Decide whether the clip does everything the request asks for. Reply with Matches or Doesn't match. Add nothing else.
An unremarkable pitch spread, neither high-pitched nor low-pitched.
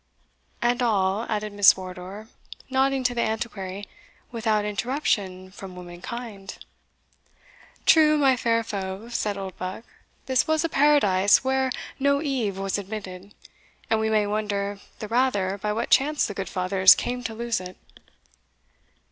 Doesn't match